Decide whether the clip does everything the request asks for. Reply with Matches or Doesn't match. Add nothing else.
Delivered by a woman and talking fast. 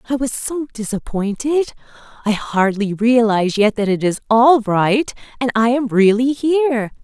Doesn't match